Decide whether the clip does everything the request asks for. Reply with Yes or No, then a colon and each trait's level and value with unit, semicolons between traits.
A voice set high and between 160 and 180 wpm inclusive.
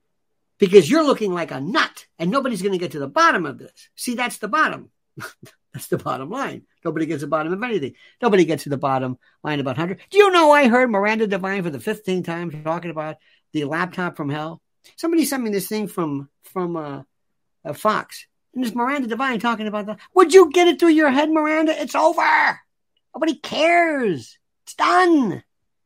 No: high, 215 Hz; average, 200 wpm